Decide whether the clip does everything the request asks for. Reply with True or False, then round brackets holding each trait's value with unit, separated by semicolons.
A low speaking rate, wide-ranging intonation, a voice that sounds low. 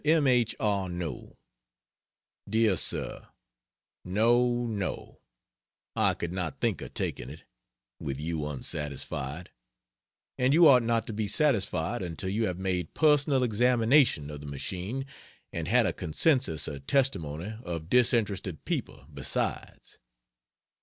True (125 wpm; 7.2 semitones; 100 Hz)